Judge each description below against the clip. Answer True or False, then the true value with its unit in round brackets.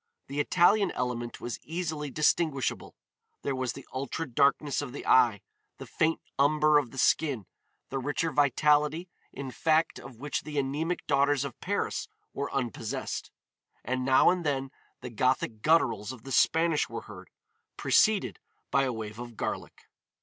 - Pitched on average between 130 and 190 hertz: True (140 Hz)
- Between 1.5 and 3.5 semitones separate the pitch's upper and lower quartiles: True (3.1 semitones)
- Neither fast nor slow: True (155 wpm)